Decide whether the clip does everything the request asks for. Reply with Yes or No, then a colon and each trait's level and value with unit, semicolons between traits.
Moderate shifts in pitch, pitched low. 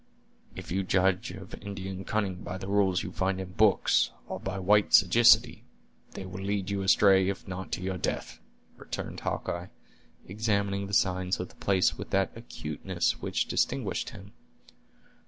No: narrow, 1.4 semitones; very low, 95 Hz